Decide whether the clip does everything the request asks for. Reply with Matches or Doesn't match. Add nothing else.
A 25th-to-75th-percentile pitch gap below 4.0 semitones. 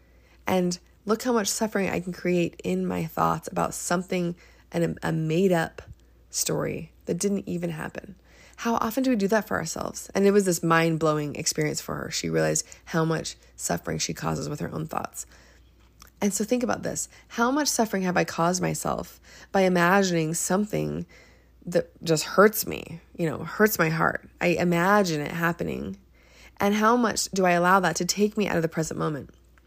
Doesn't match